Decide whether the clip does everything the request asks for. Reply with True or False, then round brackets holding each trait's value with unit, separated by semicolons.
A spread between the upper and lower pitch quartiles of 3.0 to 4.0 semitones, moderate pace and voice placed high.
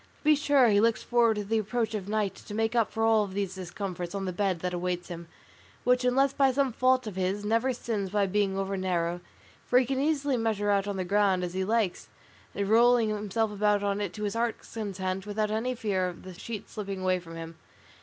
False (3.4 semitones; 230 wpm; 205 Hz)